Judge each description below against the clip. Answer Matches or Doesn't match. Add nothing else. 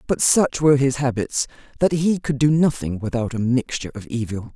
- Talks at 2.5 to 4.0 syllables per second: Doesn't match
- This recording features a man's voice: Doesn't match